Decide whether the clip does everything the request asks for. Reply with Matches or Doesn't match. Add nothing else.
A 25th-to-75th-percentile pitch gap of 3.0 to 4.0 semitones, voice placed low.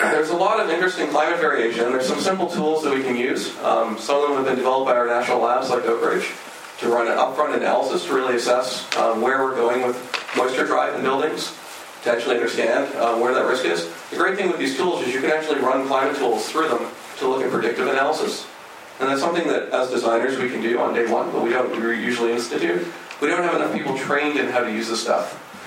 Matches